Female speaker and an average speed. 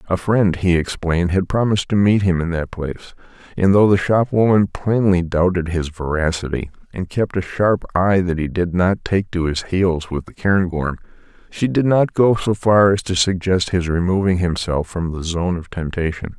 No: male; average, 195 wpm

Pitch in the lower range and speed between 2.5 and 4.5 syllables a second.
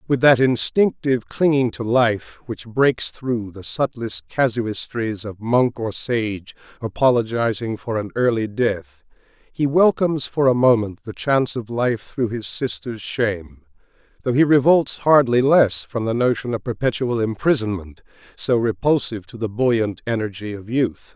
Yes: low, 115 Hz; 4.4 syllables/s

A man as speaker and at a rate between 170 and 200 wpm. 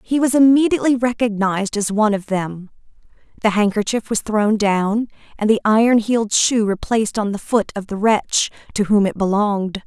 No: female; average, 175 wpm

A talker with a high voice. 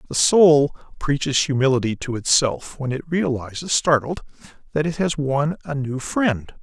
No: medium, 140 Hz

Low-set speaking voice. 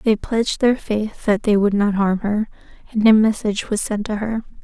No: high, 210 Hz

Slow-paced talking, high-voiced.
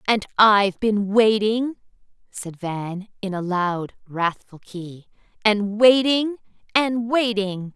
Yes: slow, 110 wpm; high, 210 Hz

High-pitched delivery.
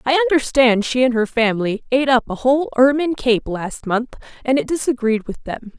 Yes: very high, 250 Hz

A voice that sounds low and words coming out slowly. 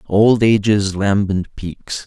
Yes: low, 100 Hz; slow, 115 wpm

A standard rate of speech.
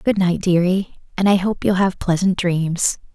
Yes: average, 190 wpm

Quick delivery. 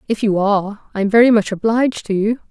Yes: fast, 215 wpm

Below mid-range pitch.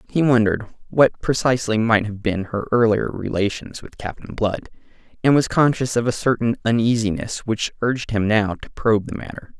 Yes: low, 115 Hz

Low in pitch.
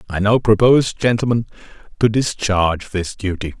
Yes: low, 105 Hz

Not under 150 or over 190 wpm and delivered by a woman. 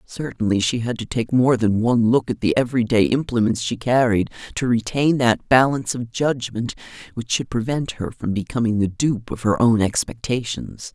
Yes: average, 185 wpm; female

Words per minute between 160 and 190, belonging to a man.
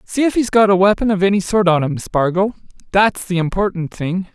No: fast, 205 wpm; male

